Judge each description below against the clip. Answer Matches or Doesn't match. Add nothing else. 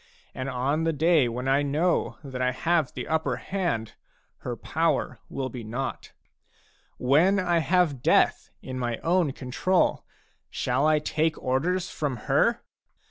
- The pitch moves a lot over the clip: Doesn't match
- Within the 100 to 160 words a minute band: Matches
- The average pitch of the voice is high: Doesn't match